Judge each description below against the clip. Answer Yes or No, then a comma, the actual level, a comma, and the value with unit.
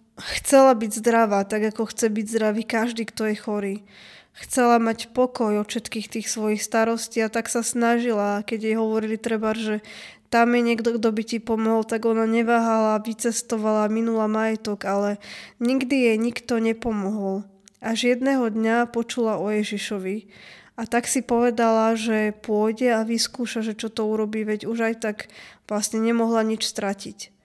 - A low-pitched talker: No, high, 225 Hz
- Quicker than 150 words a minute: Yes, average, 160 wpm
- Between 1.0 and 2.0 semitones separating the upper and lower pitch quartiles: Yes, narrow, 1.3 semitones